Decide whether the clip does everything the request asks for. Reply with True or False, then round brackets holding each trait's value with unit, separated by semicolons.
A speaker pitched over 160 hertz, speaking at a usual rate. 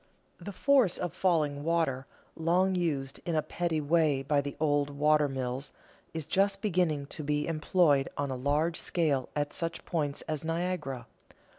False (155 Hz; 160 wpm)